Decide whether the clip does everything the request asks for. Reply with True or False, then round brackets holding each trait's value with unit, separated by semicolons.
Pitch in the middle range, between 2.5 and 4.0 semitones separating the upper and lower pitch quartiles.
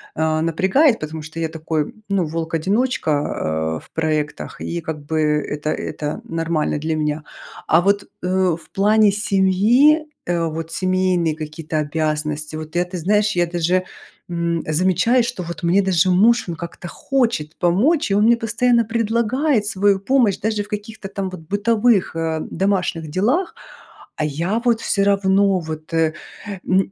False (180 Hz; 4.6 semitones)